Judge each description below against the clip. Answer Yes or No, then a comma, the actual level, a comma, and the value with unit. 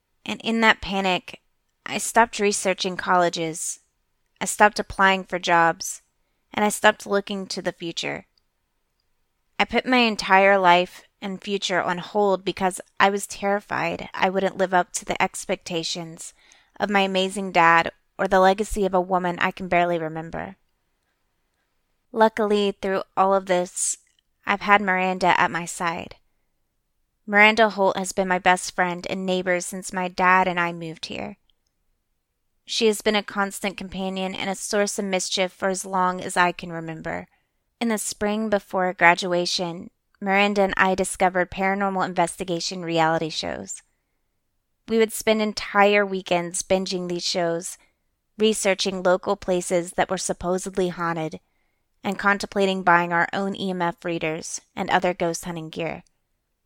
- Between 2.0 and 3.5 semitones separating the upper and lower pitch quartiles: Yes, narrow, 2.4 semitones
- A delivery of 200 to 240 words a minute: No, average, 145 wpm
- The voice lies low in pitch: No, medium, 185 Hz